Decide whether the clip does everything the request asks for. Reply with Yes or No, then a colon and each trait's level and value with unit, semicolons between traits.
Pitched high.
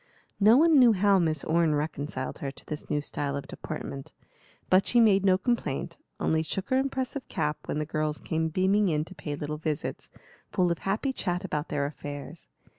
No: medium, 165 Hz